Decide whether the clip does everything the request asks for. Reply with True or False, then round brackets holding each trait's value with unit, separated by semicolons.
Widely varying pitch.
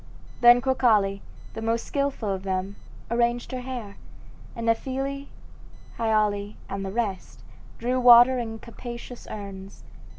False (3.5 semitones)